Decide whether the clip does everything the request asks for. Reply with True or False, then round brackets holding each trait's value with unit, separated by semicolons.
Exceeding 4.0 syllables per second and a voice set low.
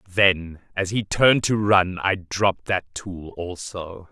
False (3.8 syllables/s; 95 Hz)